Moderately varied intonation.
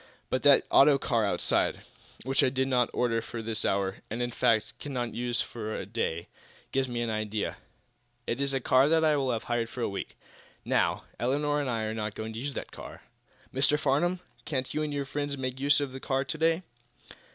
Yes: average, 3.6 semitones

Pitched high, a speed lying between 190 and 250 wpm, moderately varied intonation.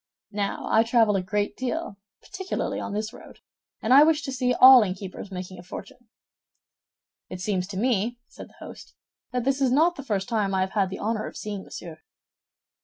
Yes: high, 215 Hz; average, 195 wpm; average, 4.7 semitones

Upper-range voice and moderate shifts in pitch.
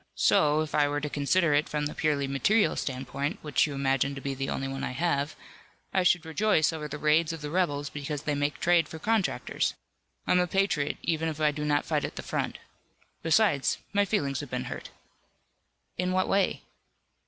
No: medium, 150 Hz; average, 3.2 semitones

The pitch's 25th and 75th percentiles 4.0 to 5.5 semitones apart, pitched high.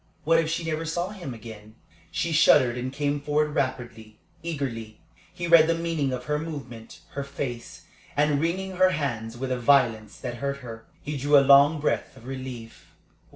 No: average, 4.6 semitones; medium, 140 Hz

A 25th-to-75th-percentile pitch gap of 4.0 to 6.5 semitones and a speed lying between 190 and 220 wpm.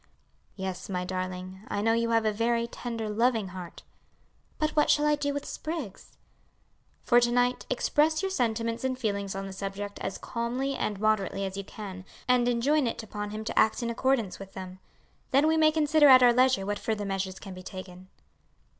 Yes: average, 4.7 semitones; average, 195 wpm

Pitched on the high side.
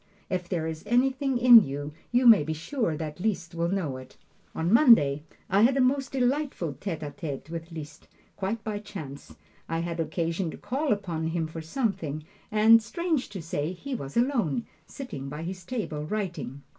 No: medium, 180 Hz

